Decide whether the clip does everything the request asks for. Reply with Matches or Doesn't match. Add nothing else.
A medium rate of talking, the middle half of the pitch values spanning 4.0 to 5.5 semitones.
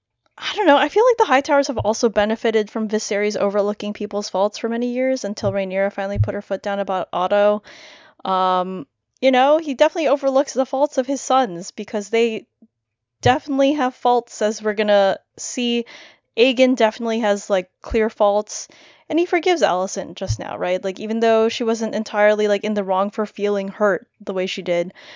Matches